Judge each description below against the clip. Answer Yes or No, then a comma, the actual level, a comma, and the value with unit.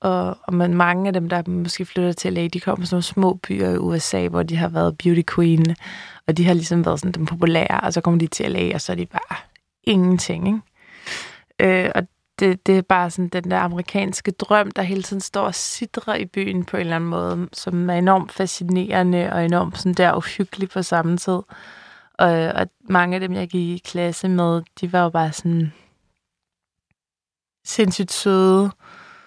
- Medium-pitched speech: Yes, medium, 180 Hz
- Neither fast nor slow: Yes, average, 195 wpm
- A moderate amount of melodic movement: No, narrow, 1.8 semitones